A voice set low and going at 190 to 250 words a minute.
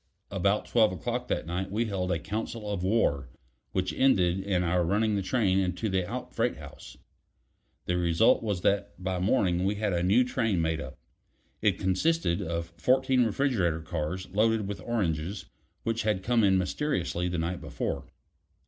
No: very low, 95 Hz; average, 170 wpm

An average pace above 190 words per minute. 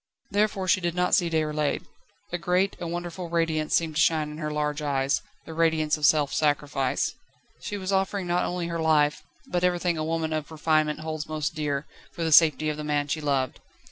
Yes: fast, 205 wpm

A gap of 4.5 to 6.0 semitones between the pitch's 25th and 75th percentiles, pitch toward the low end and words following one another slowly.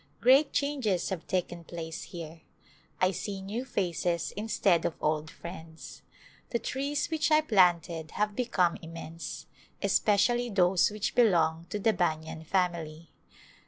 No: average, 4.8 semitones; medium, 180 Hz; slow, 130 wpm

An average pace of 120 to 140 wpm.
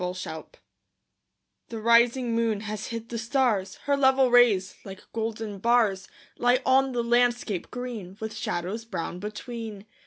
Yes: slow, 135 wpm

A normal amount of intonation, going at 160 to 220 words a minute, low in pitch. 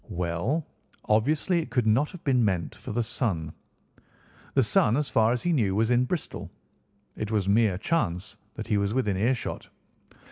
Yes: average, 4.7 semitones; average, 175 wpm; low, 115 Hz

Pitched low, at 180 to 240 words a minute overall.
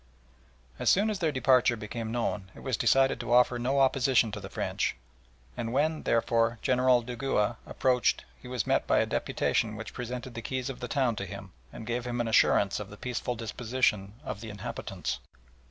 Yes: low, 120 Hz; average, 190 wpm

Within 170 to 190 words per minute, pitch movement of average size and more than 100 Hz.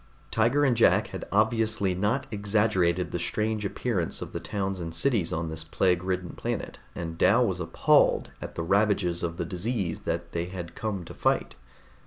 No: average, 180 wpm; average, 4.1 semitones; very low, 95 Hz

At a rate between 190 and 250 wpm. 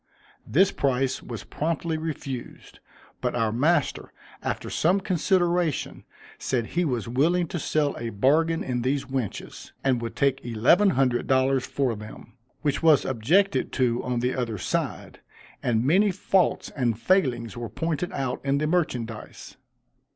No: average, 145 wpm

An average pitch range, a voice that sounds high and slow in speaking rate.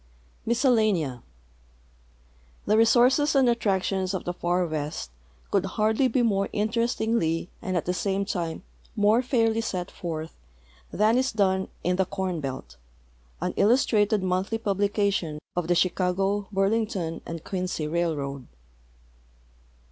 Yes: average, 4.1 semitones; high, 195 Hz; slow, 125 wpm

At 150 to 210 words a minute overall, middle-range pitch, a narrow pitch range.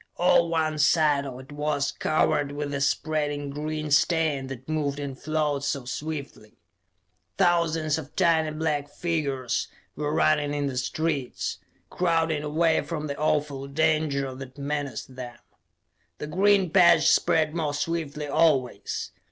No: slow, 135 wpm; medium, 150 Hz; narrow, 2.1 semitones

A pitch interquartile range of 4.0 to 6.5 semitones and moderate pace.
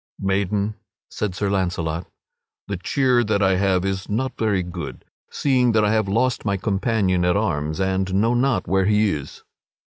No: average, 2.8 semitones; average, 170 wpm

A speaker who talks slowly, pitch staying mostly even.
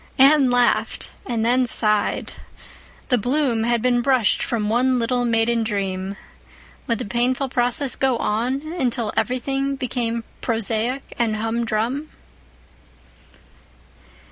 Yes: slow, 115 wpm; narrow, 2.3 semitones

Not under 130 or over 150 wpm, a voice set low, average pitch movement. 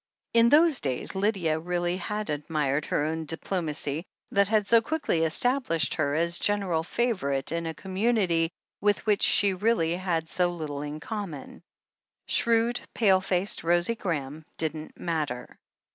No: average, 145 wpm; medium, 175 Hz; average, 4.7 semitones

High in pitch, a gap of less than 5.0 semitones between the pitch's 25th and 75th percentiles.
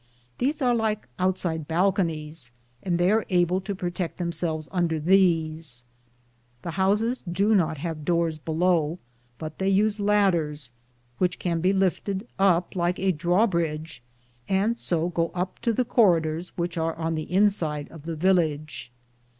No: medium, 175 Hz; average, 3.1 semitones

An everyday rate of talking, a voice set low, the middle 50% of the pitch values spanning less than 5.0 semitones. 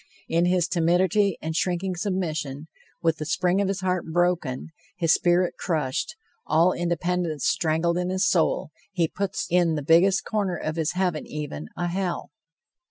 No: average, 160 wpm; medium, 175 Hz; narrow, 2.4 semitones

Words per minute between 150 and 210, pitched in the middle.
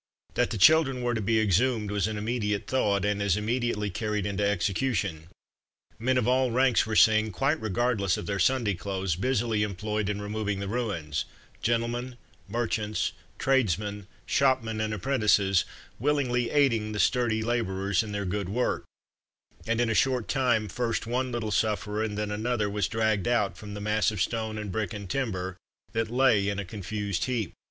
No: average, 175 wpm; low, 110 Hz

